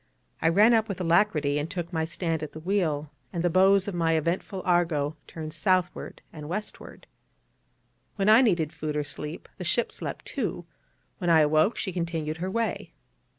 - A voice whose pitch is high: No, medium, 170 Hz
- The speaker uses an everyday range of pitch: Yes, average, 3.4 semitones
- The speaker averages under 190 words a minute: Yes, average, 180 wpm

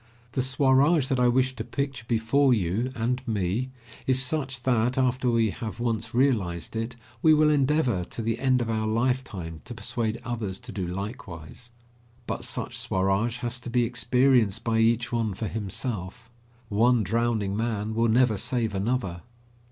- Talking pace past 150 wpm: Yes, average, 165 wpm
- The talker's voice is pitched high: No, low, 115 Hz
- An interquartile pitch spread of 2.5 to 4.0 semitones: Yes, average, 2.8 semitones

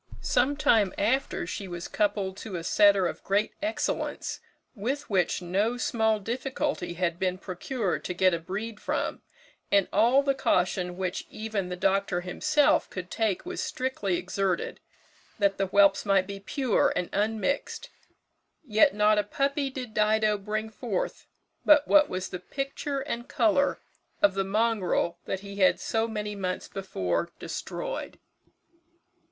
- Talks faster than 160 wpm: No, average, 150 wpm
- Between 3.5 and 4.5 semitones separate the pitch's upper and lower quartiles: Yes, average, 4.1 semitones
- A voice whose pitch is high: Yes, high, 205 Hz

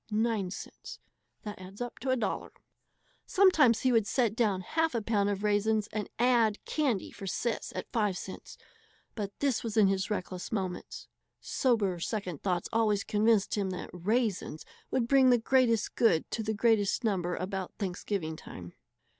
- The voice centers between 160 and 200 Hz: No, high, 210 Hz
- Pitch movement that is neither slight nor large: Yes, average, 3.3 semitones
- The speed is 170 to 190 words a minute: No, average, 140 wpm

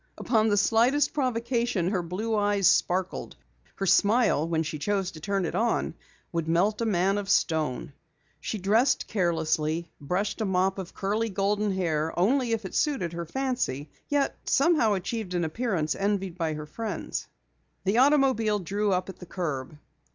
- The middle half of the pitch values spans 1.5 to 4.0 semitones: No, average, 4.7 semitones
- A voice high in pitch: Yes, high, 195 Hz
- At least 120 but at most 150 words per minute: No, average, 165 wpm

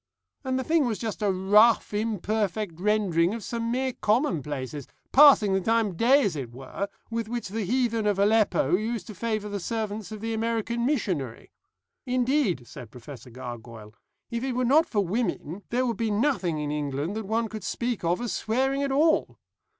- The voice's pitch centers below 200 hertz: No, high, 215 Hz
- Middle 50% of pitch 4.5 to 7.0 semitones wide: Yes, average, 4.9 semitones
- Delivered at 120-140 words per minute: No, average, 185 wpm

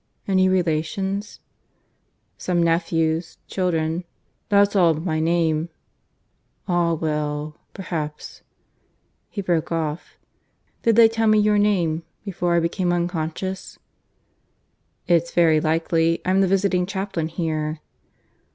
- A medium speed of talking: No, slow, 115 wpm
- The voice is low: No, medium, 170 Hz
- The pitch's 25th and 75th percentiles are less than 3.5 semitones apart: Yes, average, 3.0 semitones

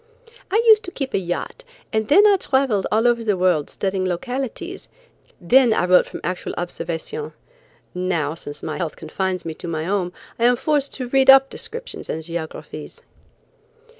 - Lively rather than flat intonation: Yes, wide, 7.4 semitones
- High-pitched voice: Yes, high, 205 Hz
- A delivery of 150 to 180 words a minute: Yes, average, 170 wpm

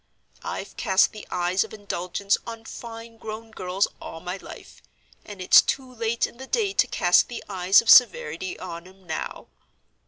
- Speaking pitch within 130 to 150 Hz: No, high, 205 Hz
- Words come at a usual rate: Yes, average, 175 wpm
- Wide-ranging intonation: No, average, 3.9 semitones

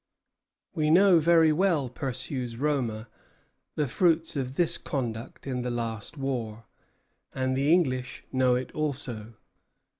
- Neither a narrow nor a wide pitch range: Yes, average, 4.0 semitones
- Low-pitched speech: Yes, low, 130 Hz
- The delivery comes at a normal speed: No, slow, 125 wpm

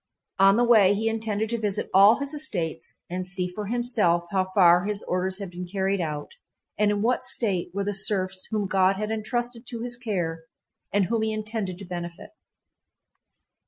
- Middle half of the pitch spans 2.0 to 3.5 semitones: Yes, average, 3.2 semitones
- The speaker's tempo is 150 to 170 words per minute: No, average, 185 wpm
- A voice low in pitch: No, high, 200 Hz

